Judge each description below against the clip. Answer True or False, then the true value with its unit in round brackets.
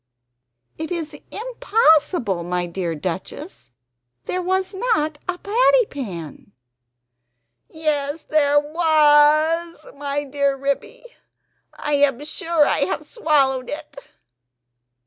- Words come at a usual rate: False (100 wpm)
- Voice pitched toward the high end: True (295 Hz)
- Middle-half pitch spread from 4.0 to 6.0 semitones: False (3.3 semitones)